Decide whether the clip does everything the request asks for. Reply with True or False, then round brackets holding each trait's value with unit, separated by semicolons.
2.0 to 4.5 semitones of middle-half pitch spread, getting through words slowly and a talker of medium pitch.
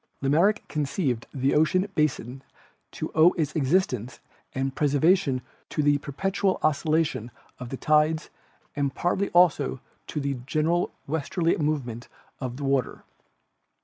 True (3.5 semitones; 125 wpm; 150 Hz)